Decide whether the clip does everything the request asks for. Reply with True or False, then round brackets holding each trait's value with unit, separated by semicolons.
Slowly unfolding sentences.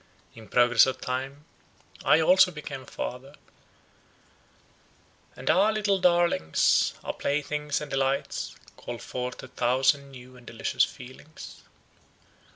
True (120 wpm)